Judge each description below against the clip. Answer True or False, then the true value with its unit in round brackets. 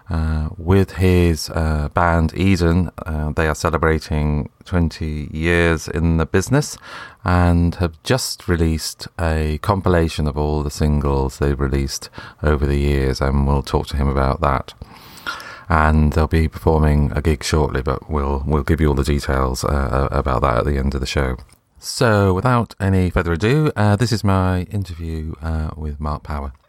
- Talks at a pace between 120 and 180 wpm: True (170 wpm)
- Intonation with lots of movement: False (3.3 semitones)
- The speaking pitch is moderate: False (80 Hz)